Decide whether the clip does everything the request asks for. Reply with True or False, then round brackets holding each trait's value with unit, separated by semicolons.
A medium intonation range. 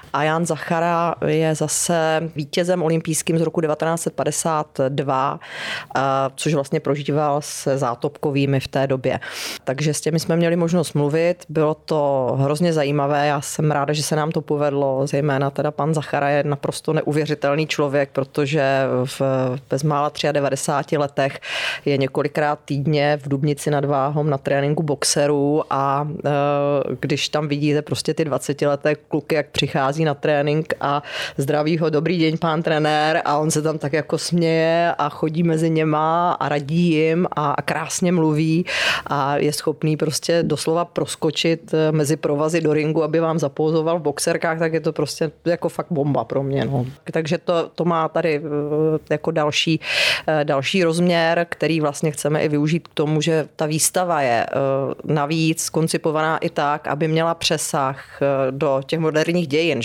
False (2.1 semitones)